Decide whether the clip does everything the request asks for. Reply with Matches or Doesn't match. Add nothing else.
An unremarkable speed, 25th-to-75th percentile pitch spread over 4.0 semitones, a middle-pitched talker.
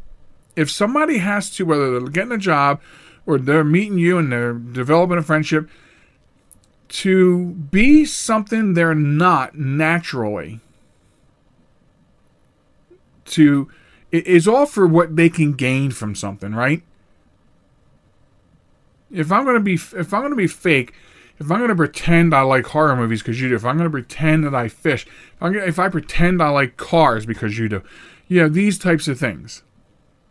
Matches